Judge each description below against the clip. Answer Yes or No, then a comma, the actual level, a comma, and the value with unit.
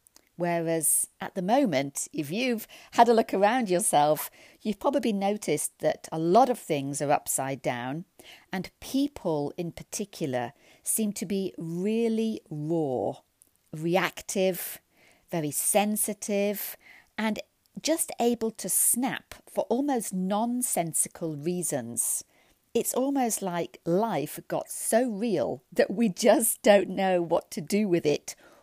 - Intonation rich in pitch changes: Yes, wide, 5.7 semitones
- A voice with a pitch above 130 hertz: Yes, high, 190 Hz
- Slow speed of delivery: Yes, slow, 125 wpm